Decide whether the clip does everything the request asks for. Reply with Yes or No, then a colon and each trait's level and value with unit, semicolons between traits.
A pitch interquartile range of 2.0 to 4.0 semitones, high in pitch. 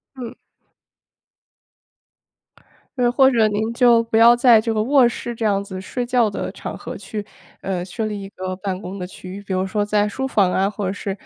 Yes: average, 3.4 semitones; high, 210 Hz